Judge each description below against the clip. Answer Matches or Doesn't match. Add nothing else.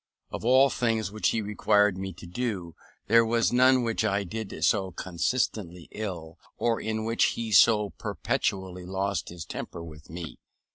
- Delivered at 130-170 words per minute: Matches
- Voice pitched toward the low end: Matches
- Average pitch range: Matches